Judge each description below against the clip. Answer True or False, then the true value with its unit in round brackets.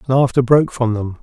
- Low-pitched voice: True (125 Hz)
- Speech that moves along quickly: False (195 wpm)